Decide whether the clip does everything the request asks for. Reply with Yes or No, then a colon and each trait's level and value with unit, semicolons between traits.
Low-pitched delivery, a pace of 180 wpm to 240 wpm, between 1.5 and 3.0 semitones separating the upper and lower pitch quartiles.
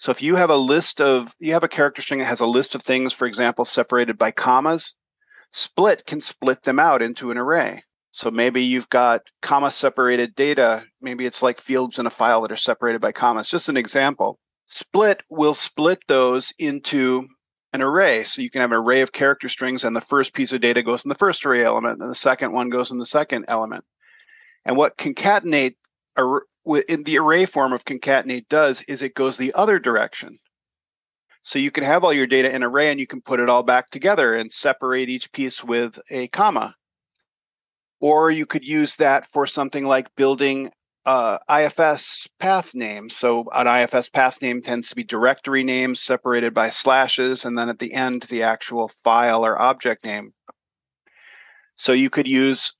Yes: low, 130 Hz; average, 195 wpm; average, 2.7 semitones